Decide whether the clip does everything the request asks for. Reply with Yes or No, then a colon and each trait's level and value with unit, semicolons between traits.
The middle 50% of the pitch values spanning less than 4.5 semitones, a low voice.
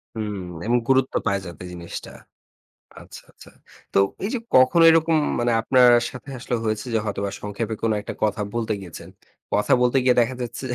Yes: average, 3.8 semitones; low, 115 Hz